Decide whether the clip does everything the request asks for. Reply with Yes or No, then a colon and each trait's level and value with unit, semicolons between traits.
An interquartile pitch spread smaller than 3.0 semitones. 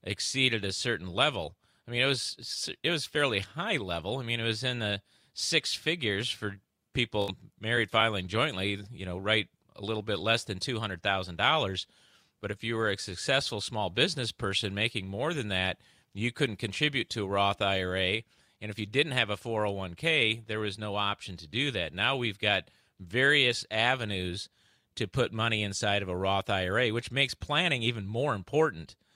No: average, 3.3 semitones